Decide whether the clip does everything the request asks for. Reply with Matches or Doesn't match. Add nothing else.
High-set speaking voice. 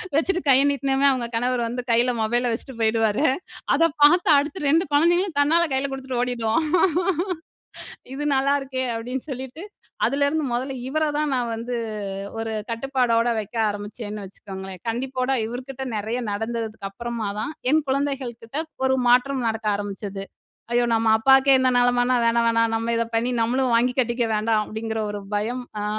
Matches